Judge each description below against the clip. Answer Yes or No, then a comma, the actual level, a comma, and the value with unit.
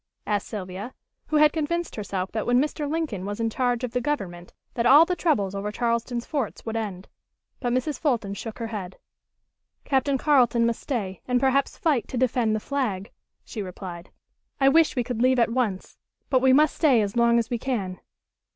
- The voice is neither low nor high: No, high, 240 Hz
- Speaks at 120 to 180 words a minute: No, average, 195 wpm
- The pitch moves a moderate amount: Yes, average, 4.5 semitones